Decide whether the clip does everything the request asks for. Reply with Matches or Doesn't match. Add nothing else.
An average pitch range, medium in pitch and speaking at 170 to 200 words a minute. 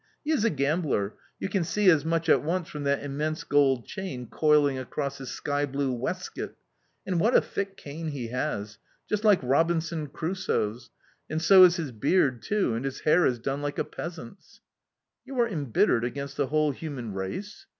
Matches